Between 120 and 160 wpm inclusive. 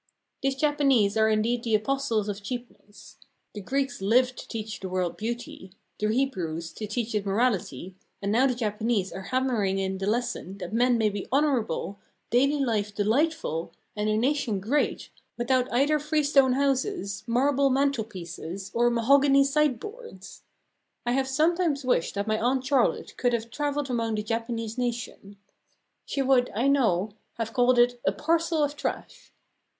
Yes: average, 155 wpm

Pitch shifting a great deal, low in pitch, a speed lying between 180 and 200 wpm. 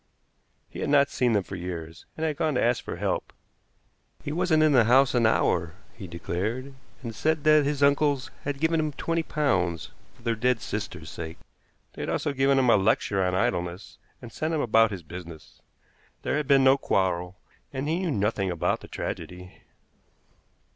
Yes: wide, 7.6 semitones; low, 120 Hz; average, 190 wpm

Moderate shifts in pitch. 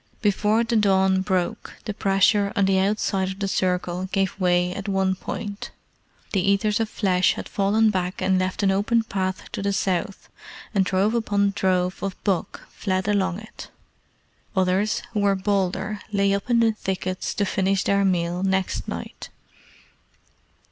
No: narrow, 1.5 semitones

